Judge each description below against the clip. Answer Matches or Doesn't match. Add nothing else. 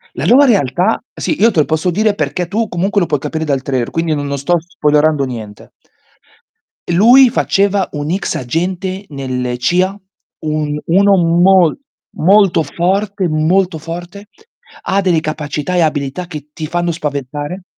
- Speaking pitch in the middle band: Matches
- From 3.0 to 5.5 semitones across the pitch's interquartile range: Matches